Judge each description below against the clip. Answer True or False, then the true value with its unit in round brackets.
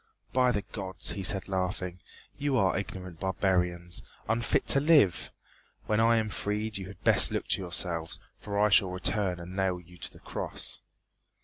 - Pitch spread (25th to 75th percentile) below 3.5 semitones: True (2.8 semitones)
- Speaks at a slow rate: False (175 wpm)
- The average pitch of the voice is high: False (95 Hz)